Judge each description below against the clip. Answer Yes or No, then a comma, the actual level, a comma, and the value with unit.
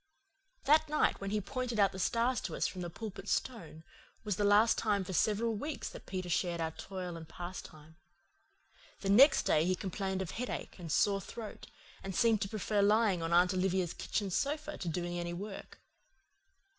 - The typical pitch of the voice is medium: No, high, 195 Hz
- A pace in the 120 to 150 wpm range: No, average, 185 wpm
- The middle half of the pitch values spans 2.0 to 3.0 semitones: No, average, 3.7 semitones